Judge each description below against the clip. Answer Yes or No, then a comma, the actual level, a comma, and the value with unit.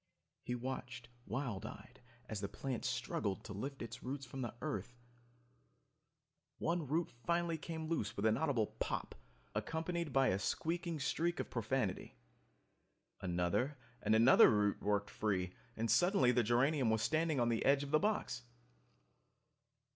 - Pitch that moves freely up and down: Yes, wide, 6.0 semitones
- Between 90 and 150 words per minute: Yes, average, 145 wpm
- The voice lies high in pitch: No, low, 125 Hz